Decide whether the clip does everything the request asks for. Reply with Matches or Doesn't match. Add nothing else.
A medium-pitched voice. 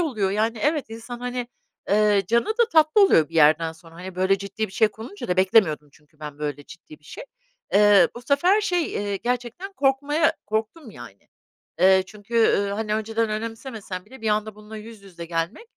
Doesn't match